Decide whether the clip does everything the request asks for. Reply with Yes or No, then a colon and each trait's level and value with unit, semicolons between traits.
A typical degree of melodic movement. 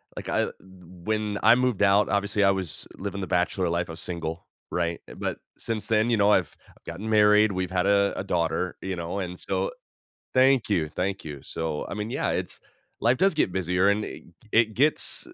Yes: average, 3.2 semitones